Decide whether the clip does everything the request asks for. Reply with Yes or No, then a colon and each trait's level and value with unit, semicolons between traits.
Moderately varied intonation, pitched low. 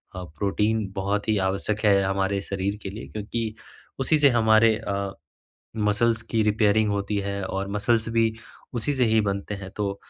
No: narrow, 2.1 semitones; low, 105 Hz